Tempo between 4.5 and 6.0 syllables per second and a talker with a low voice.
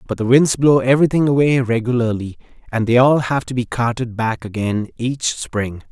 Yes: 5.1 syllables/s; low, 125 Hz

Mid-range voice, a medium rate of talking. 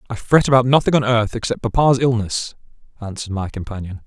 No: low, 115 Hz; average, 175 wpm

